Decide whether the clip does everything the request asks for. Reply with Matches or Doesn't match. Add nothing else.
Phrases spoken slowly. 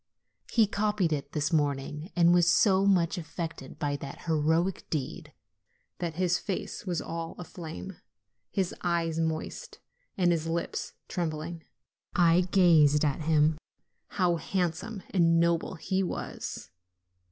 Matches